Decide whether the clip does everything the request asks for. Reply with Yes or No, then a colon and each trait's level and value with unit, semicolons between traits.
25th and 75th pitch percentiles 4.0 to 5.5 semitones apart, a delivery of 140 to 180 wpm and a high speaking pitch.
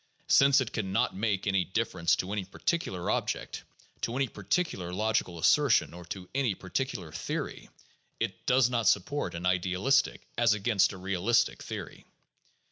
No: average, 4.7 semitones; average, 160 wpm; low, 100 Hz